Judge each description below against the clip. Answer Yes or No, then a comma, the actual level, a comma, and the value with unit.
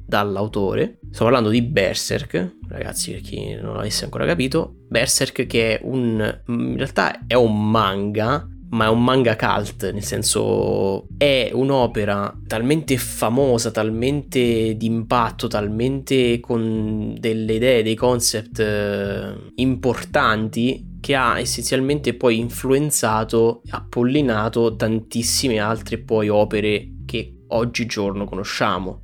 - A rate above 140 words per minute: No, slow, 115 wpm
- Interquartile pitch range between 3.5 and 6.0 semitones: No, average, 2.9 semitones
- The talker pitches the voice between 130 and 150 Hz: No, low, 115 Hz